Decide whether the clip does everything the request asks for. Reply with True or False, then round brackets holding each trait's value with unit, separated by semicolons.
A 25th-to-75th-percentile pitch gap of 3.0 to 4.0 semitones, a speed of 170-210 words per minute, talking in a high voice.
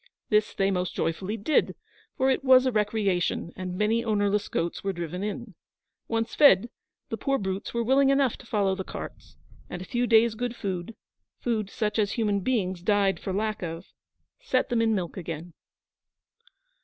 True (3.7 semitones; 175 wpm; 210 Hz)